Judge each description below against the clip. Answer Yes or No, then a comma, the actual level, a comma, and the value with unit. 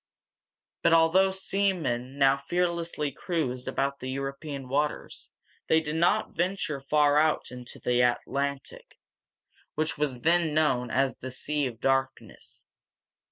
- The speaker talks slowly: Yes, slow, 125 wpm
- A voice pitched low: No, medium, 145 Hz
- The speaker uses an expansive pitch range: No, average, 3.6 semitones